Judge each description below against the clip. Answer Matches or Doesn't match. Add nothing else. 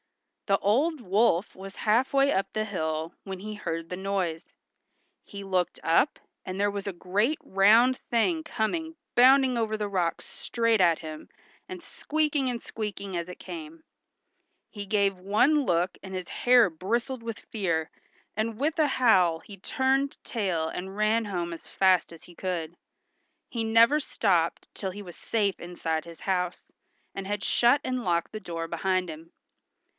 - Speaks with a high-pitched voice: Matches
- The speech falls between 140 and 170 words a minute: Matches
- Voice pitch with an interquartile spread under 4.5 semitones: Doesn't match